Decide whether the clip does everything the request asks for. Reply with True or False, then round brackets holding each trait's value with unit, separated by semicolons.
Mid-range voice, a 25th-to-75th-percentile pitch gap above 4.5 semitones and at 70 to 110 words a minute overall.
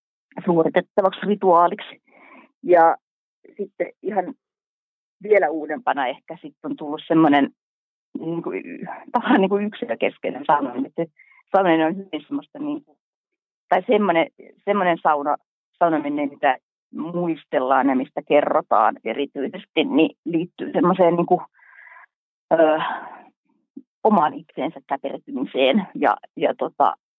True (175 Hz; 5.6 semitones; 105 wpm)